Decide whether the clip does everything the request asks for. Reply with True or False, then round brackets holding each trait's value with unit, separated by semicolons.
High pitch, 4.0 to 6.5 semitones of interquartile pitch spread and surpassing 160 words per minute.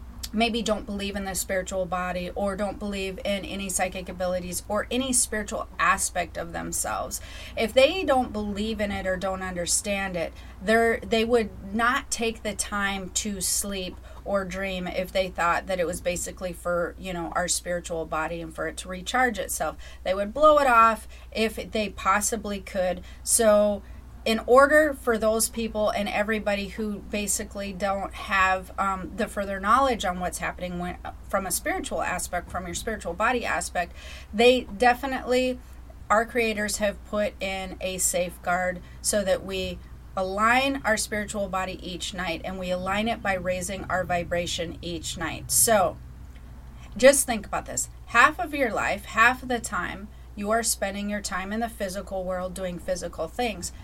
False (200 Hz; 3.5 semitones; 170 wpm)